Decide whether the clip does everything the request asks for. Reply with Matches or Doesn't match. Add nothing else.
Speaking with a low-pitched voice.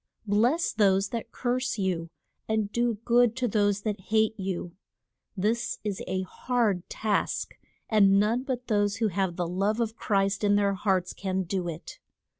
Doesn't match